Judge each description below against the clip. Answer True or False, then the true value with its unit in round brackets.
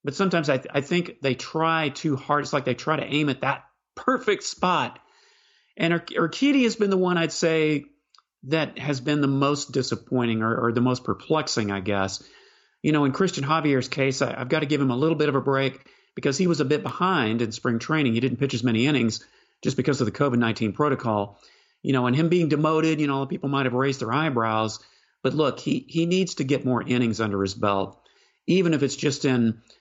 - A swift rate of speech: True (225 wpm)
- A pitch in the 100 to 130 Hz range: False (140 Hz)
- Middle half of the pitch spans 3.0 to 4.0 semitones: False (4.4 semitones)